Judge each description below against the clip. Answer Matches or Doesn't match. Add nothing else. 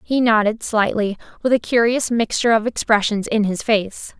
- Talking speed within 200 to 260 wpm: Doesn't match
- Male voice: Doesn't match